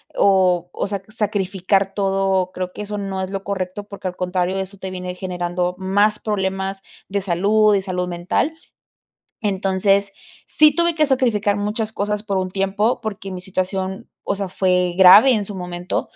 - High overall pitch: Yes, high, 195 Hz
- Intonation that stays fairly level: Yes, narrow, 1.8 semitones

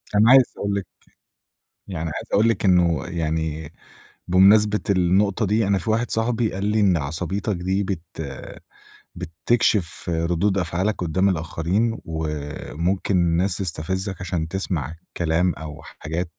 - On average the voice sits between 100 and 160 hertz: No, very low, 90 Hz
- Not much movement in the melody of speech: No, average, 3.5 semitones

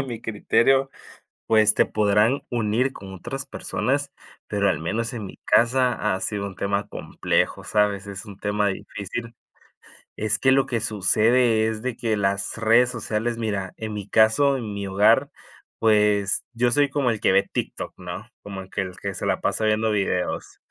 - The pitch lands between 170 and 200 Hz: No, low, 110 Hz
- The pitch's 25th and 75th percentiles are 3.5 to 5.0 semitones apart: No, average, 2.9 semitones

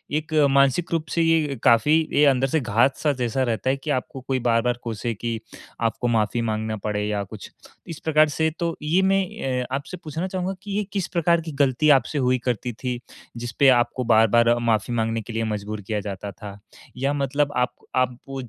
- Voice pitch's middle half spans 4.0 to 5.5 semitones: Yes, average, 4.9 semitones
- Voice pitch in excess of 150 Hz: No, low, 125 Hz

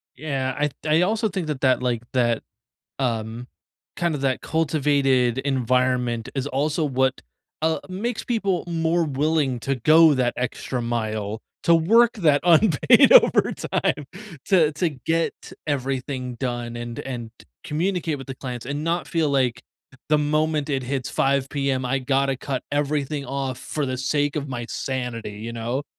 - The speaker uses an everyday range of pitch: Yes, average, 3.5 semitones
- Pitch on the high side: No, low, 135 Hz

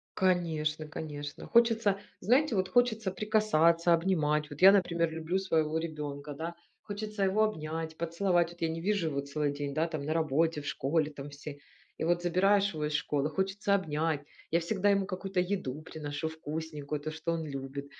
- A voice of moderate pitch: Yes, medium, 165 Hz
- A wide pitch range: No, average, 4.0 semitones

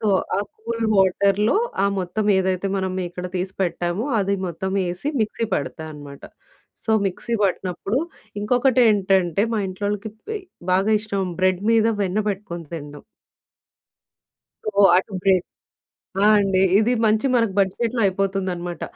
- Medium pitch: No, high, 195 Hz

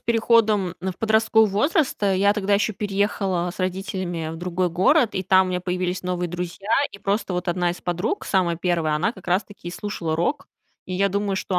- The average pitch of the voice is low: No, high, 190 Hz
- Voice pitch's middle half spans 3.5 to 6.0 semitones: No, narrow, 2.5 semitones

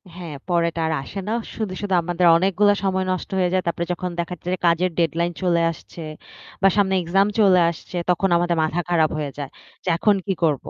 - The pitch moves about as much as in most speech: No, narrow, 2.1 semitones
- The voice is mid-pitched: Yes, medium, 175 Hz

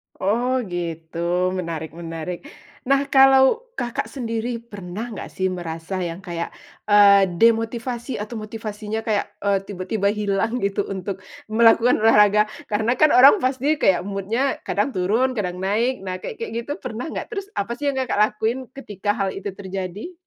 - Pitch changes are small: No, average, 4.2 semitones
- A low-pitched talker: No, high, 210 Hz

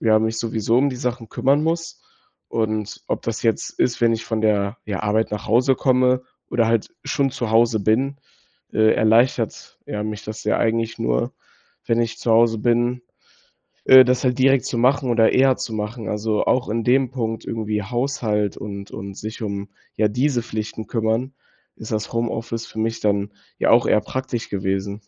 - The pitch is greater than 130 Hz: No, low, 115 Hz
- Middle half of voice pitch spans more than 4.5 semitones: No, narrow, 2.6 semitones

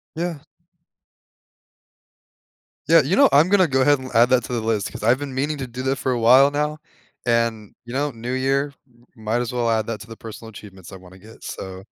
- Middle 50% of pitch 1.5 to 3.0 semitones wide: No, average, 3.6 semitones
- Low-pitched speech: Yes, low, 125 Hz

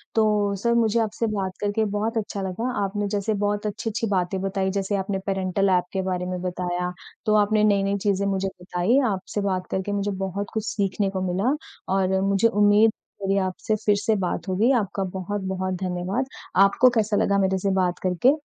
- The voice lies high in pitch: Yes, high, 200 Hz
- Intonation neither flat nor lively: No, narrow, 2.0 semitones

